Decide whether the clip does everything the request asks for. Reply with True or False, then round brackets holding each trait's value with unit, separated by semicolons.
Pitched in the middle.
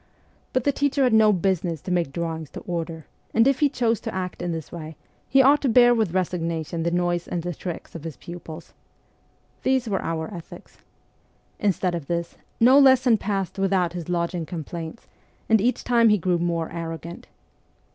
True (180 Hz)